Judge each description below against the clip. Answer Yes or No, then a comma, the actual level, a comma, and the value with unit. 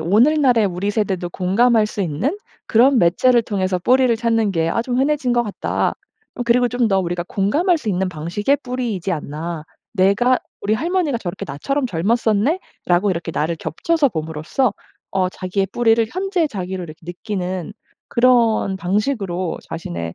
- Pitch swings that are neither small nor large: No, wide, 5.7 semitones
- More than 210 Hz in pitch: No, high, 205 Hz